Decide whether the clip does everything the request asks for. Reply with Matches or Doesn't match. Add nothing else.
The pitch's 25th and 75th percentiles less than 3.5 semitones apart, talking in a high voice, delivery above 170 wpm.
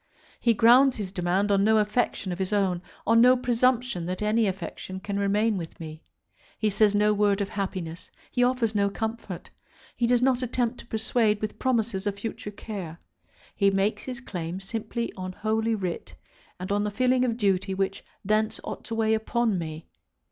Matches